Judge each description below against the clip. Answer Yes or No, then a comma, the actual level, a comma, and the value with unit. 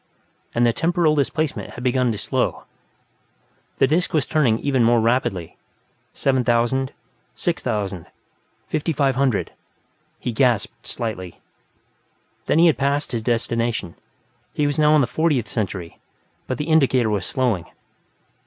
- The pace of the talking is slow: Yes, slow, 130 wpm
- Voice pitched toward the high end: No, low, 125 Hz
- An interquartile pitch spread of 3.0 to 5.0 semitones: Yes, average, 4.3 semitones